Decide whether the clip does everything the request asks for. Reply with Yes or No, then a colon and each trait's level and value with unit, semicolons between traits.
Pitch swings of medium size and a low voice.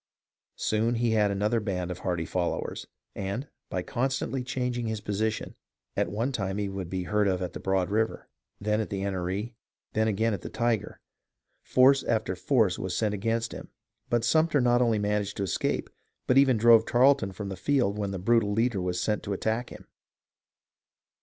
Yes: average, 3.5 semitones; low, 105 Hz